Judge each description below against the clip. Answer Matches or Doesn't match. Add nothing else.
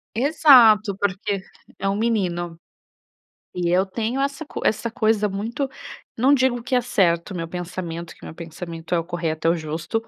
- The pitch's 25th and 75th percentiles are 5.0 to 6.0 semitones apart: Matches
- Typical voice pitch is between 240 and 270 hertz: Doesn't match